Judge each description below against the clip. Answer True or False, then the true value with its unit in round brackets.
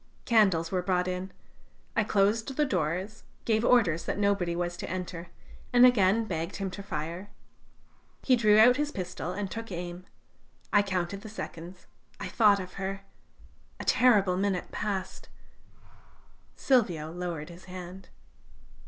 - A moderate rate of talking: True (145 wpm)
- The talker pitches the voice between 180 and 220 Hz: True (190 Hz)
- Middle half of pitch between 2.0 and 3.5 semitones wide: True (3.2 semitones)